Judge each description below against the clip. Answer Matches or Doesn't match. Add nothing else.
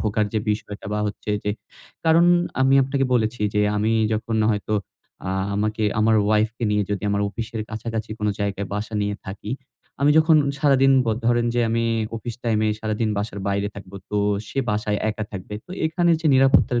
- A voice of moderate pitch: Doesn't match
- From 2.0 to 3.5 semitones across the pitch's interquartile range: Matches